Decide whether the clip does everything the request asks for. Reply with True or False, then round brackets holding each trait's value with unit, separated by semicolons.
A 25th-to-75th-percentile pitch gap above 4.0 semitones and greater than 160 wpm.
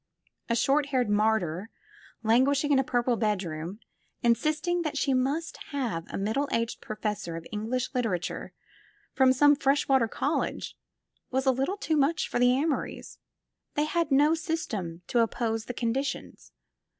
False (4.5 semitones; 155 wpm)